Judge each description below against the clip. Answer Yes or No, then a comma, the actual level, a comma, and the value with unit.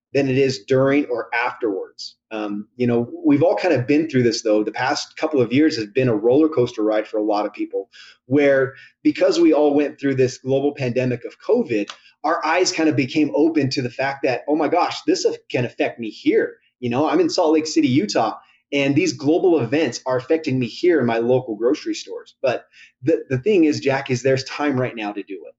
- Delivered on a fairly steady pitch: No, average, 4.6 semitones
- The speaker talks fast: Yes, fast, 225 wpm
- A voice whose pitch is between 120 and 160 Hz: Yes, medium, 140 Hz